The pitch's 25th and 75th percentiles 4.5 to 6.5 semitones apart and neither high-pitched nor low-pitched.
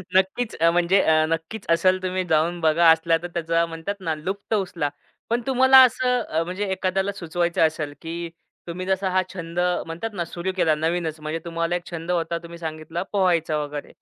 No: narrow, 2.5 semitones; medium, 170 Hz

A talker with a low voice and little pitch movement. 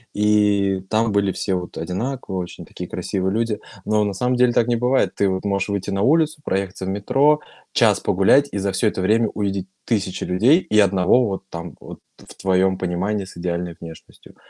No: low, 100 Hz; average, 3.2 semitones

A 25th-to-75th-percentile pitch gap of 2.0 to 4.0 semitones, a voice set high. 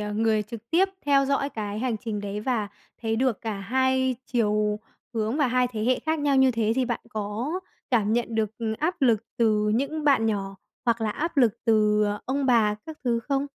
Yes: average, 3.7 semitones; high, 230 Hz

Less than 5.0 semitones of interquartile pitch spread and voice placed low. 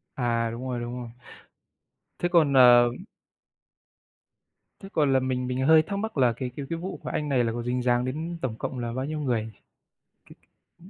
Yes: average, 3.8 semitones; low, 130 Hz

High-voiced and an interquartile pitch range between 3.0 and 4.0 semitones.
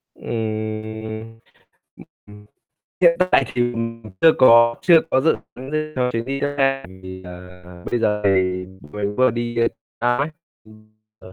No: low, 115 Hz; average, 3.7 semitones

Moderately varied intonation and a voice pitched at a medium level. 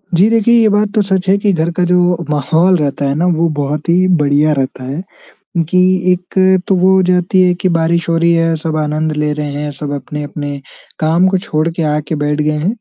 Yes: average, 3.5 semitones; medium, 165 Hz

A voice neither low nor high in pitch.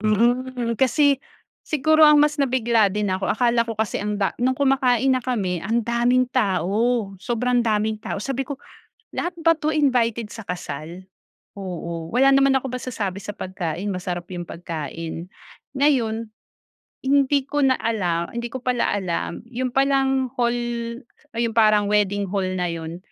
No: high, 235 Hz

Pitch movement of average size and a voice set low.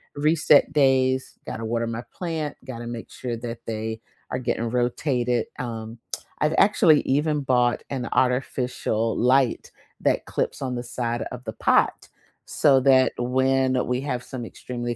No: narrow, 2.1 semitones; low, 125 Hz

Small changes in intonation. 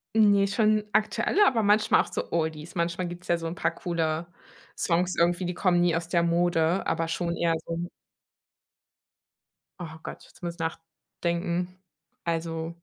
Yes: narrow, 1.6 semitones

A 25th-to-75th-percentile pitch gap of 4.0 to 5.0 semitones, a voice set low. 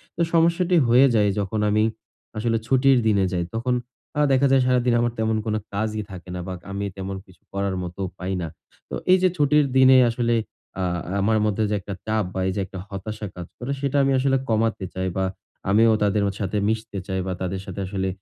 Yes: average, 4.5 semitones; low, 110 Hz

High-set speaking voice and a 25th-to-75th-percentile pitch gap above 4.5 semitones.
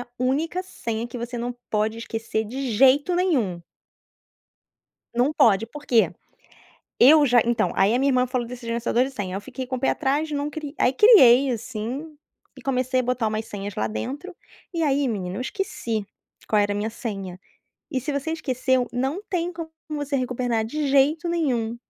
No: very high, 255 Hz; average, 4.2 semitones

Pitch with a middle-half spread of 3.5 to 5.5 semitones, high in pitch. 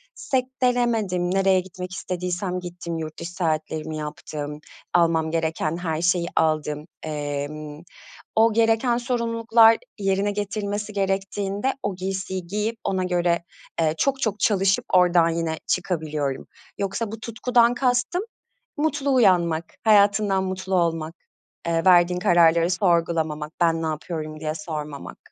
No: average, 4.2 semitones; medium, 180 Hz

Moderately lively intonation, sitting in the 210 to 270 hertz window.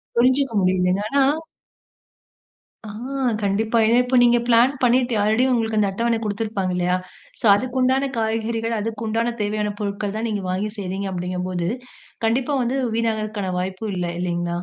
Yes: average, 3.3 semitones; high, 220 Hz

